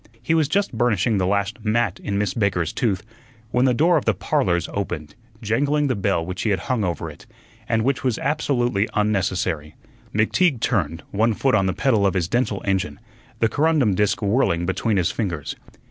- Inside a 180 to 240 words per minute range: Yes, average, 190 wpm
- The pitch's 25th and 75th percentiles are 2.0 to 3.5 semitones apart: No, average, 4.8 semitones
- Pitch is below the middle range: Yes, low, 105 Hz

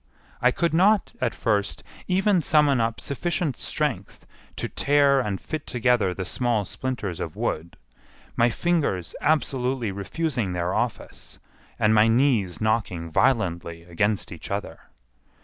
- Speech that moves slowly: Yes, slow, 130 wpm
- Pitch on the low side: Yes, low, 120 Hz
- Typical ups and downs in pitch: No, wide, 6.5 semitones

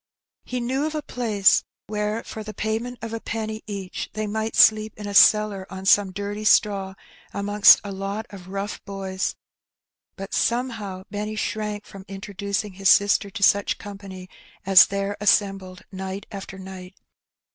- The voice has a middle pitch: No, high, 205 Hz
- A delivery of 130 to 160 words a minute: Yes, average, 155 wpm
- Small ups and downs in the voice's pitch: Yes, narrow, 1.8 semitones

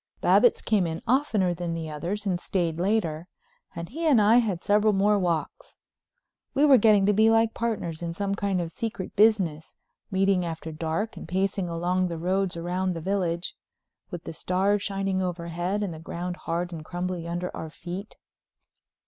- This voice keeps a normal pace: Yes, average, 175 wpm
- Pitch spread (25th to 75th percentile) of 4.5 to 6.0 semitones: No, average, 3.3 semitones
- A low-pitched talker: No, medium, 185 Hz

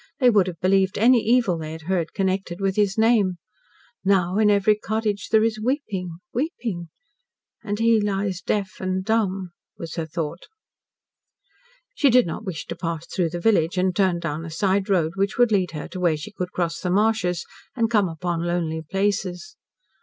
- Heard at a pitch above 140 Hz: Yes, high, 190 Hz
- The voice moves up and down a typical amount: Yes, average, 3.6 semitones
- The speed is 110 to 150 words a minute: No, average, 185 wpm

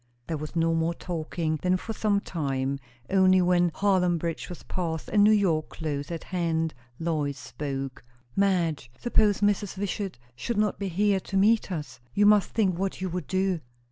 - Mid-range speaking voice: Yes, medium, 180 Hz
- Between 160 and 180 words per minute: Yes, average, 175 wpm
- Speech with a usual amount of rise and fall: Yes, average, 3.6 semitones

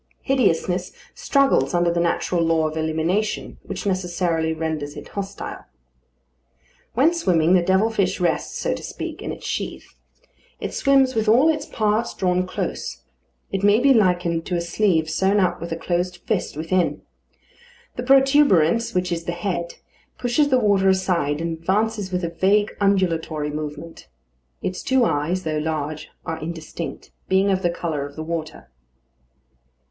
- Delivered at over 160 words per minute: No, average, 155 wpm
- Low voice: No, medium, 180 Hz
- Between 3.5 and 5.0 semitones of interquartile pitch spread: Yes, average, 4.1 semitones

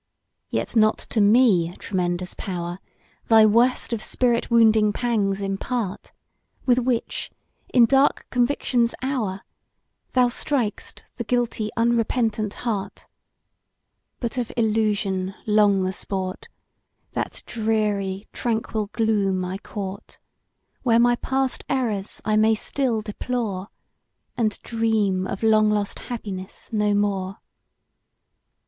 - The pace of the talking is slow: Yes, slow, 110 wpm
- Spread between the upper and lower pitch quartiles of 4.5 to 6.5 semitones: No, average, 3.1 semitones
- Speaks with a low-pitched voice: No, high, 215 Hz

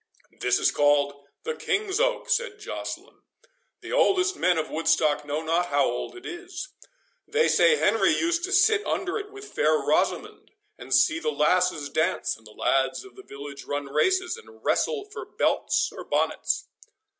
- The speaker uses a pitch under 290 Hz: No, very high, 330 Hz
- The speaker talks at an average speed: Yes, average, 170 wpm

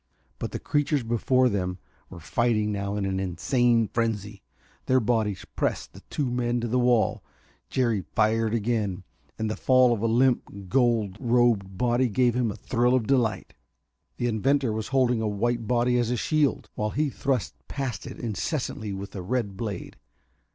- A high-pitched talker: No, low, 115 Hz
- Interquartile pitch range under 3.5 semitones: Yes, average, 3.0 semitones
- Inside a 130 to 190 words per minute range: Yes, average, 170 wpm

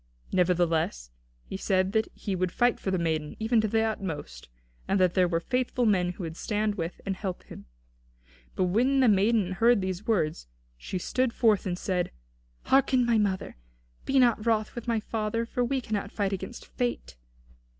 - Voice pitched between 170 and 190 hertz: No, high, 200 Hz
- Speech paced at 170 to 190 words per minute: Yes, average, 180 wpm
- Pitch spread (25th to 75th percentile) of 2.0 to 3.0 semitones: No, average, 4.2 semitones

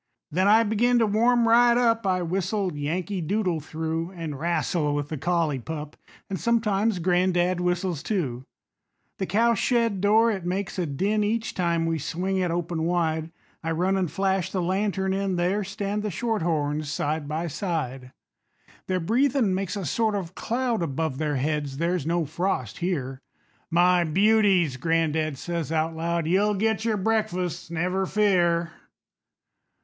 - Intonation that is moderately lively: Yes, average, 4.0 semitones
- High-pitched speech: No, medium, 180 Hz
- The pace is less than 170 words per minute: Yes, average, 155 wpm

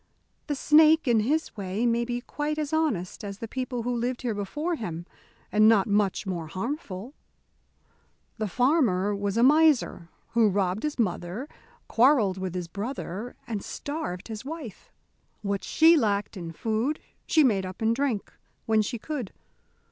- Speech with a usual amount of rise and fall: No, wide, 5.7 semitones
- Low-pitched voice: No, high, 225 Hz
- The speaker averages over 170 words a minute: No, average, 160 wpm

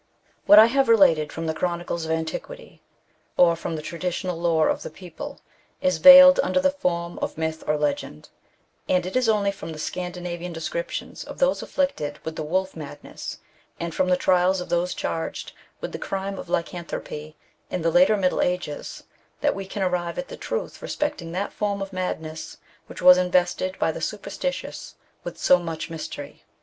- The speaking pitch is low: No, medium, 180 Hz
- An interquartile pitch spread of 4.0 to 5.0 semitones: No, average, 3.3 semitones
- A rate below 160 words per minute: No, average, 180 wpm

